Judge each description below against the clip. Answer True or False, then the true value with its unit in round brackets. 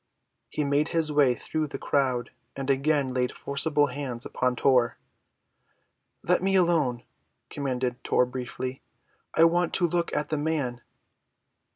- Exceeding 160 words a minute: False (140 wpm)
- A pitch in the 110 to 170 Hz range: True (140 Hz)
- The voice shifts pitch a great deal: False (3.7 semitones)